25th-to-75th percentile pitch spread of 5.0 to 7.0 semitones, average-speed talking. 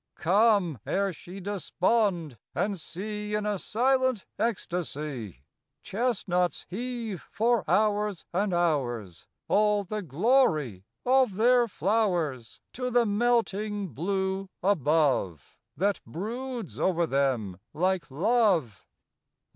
No: wide, 5.4 semitones; slow, 100 wpm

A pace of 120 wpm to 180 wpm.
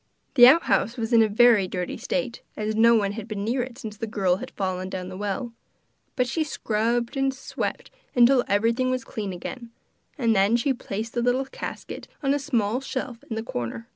No: average, 200 wpm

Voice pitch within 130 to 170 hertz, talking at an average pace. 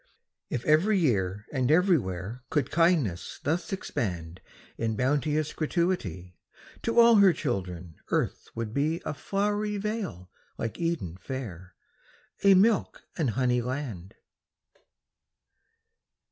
No: low, 135 Hz; slow, 110 wpm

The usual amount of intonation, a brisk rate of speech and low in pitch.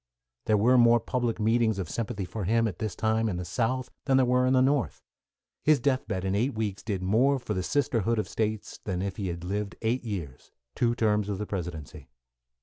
Yes: average, 3.8 semitones; fast, 220 wpm; low, 110 Hz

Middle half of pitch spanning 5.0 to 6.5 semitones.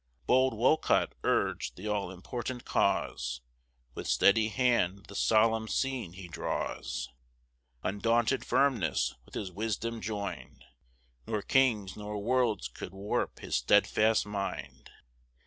No: average, 3.3 semitones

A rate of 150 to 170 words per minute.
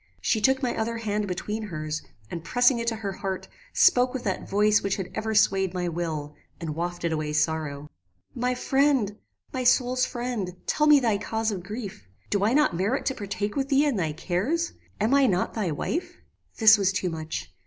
No: average, 195 wpm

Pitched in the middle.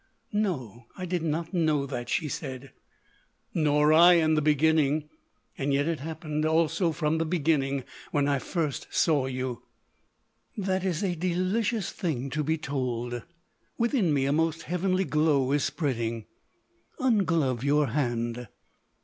Yes: medium, 155 Hz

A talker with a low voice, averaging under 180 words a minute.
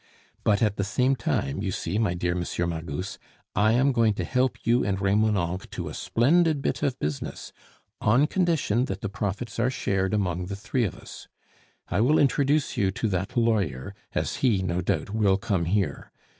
No: low, 105 Hz; average, 185 wpm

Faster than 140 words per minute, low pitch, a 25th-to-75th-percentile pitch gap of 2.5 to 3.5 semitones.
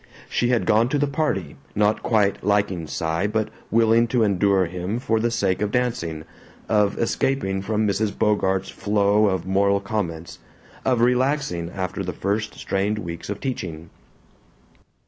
Yes: average, 150 wpm; low, 105 Hz; average, 3.2 semitones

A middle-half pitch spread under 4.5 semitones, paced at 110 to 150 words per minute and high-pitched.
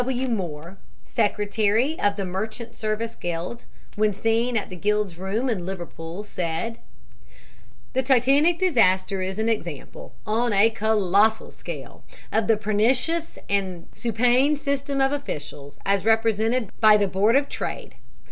Yes: average, 3.9 semitones; average, 140 wpm; high, 215 Hz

